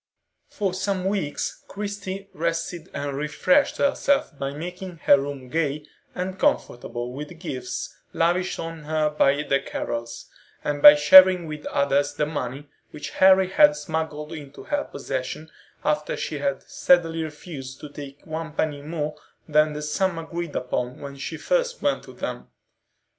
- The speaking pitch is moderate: Yes, medium, 155 Hz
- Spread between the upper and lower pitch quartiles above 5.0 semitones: No, average, 4.0 semitones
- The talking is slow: No, average, 155 wpm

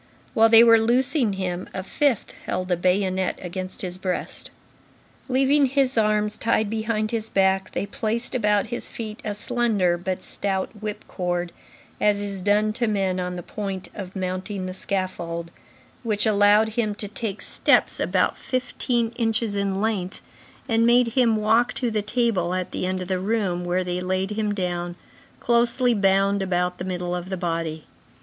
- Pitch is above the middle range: Yes, high, 205 Hz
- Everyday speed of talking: Yes, average, 170 wpm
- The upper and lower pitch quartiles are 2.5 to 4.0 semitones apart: Yes, average, 3.3 semitones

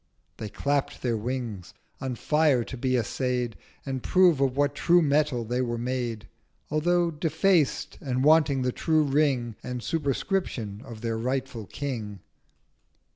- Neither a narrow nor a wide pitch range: Yes, average, 4.0 semitones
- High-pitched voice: No, low, 130 Hz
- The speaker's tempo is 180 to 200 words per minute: No, average, 140 wpm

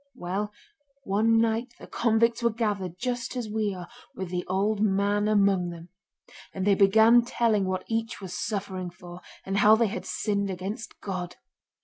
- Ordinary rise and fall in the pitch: Yes, average, 3.0 semitones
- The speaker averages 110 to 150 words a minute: No, average, 165 wpm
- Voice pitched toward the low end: No, high, 205 Hz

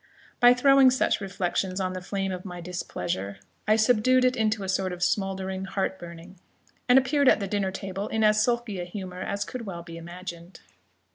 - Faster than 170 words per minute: Yes, average, 195 wpm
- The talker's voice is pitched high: Yes, high, 195 Hz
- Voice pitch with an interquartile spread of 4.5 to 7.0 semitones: No, average, 3.4 semitones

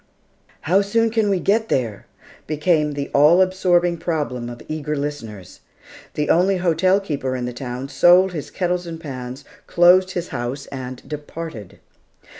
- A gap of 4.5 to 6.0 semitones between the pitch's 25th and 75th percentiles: Yes, wide, 5.4 semitones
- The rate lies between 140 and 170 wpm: Yes, average, 150 wpm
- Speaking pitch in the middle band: Yes, medium, 155 Hz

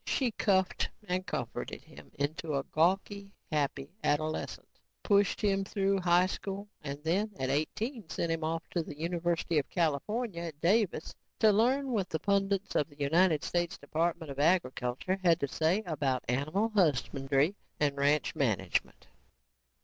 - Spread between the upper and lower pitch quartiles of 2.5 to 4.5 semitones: No, average, 5.2 semitones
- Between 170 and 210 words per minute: No, average, 150 wpm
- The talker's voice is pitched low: No, medium, 170 Hz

